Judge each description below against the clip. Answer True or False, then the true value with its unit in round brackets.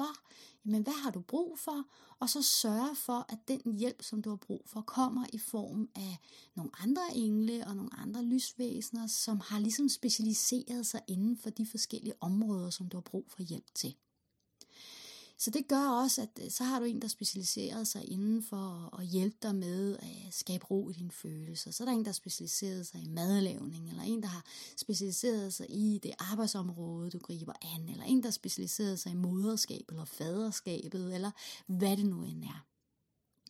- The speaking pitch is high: True (215 Hz)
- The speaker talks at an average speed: True (190 wpm)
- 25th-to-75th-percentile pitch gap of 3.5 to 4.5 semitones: True (4.2 semitones)